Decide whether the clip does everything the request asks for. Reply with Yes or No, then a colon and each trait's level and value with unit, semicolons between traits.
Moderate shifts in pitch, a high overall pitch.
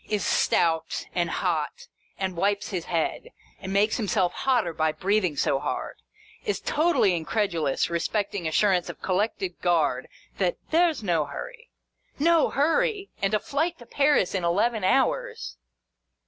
No: wide, 7.8 semitones; high, 195 Hz